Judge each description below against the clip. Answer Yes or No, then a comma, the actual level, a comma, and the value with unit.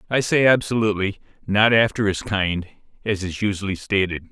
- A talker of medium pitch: No, low, 100 Hz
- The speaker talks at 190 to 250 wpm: No, average, 155 wpm